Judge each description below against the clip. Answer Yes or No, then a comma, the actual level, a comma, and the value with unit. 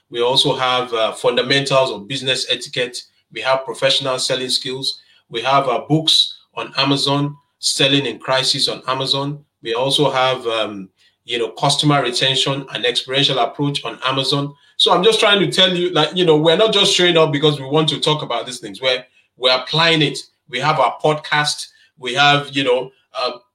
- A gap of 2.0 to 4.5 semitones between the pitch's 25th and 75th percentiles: Yes, average, 2.9 semitones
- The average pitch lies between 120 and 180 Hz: Yes, medium, 140 Hz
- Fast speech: No, average, 190 wpm